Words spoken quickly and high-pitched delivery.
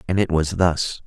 No: fast, 225 wpm; very low, 85 Hz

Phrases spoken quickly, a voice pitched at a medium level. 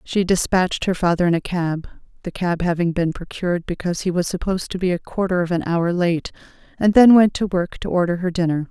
Yes: fast, 230 wpm; medium, 180 Hz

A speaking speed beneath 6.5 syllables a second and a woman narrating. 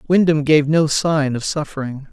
No: 4.7 syllables/s; male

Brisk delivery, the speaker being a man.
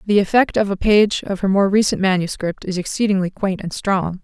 No: fast, 210 wpm; female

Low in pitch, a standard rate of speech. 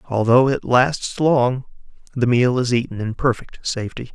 Yes: low, 125 Hz; average, 160 wpm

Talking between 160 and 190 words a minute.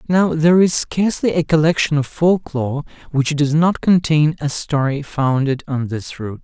Yes: average, 175 wpm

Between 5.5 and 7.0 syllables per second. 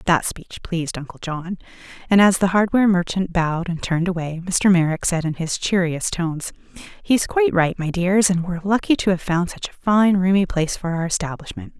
Yes: 5.6 syllables/s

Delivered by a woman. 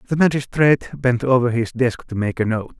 No: male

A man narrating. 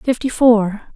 No: female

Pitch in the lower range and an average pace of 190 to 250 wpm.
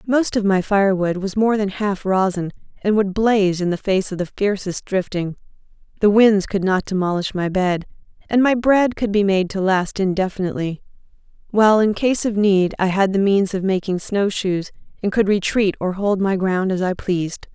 No: high, 195 Hz; average, 195 wpm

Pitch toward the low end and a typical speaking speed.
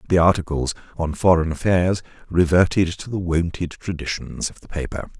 Yes: very low, 85 Hz; average, 150 wpm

